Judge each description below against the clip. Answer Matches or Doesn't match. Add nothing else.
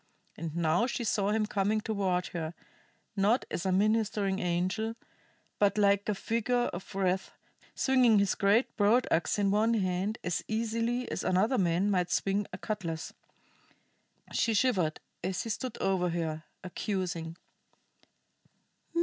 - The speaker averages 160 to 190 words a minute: Doesn't match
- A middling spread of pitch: Matches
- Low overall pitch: Doesn't match